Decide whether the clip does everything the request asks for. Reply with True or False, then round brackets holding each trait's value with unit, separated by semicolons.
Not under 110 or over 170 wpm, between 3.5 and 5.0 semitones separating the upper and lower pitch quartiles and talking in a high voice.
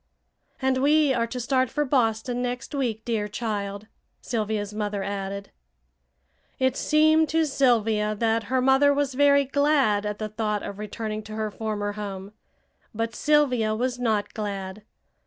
True (150 wpm; 4.0 semitones; 225 Hz)